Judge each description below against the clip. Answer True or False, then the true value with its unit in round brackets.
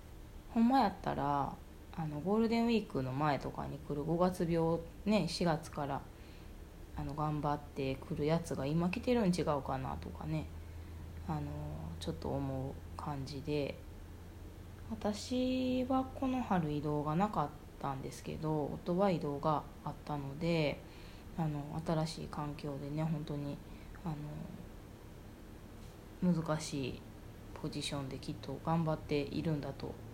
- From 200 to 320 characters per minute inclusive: True (255 characters per minute)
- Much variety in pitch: True (7.5 semitones)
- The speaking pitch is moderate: True (145 Hz)